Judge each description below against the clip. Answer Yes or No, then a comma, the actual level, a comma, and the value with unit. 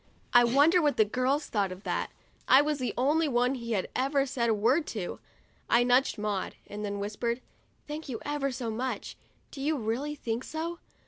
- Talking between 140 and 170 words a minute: No, average, 200 wpm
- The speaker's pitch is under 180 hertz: No, very high, 255 Hz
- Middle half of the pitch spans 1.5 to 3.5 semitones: No, average, 4.4 semitones